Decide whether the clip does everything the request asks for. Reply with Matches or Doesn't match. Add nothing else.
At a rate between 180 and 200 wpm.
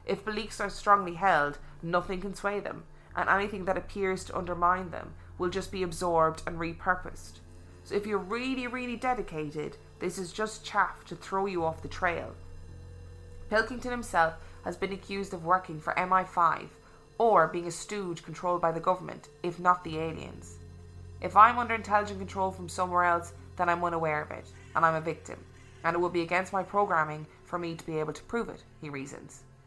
Matches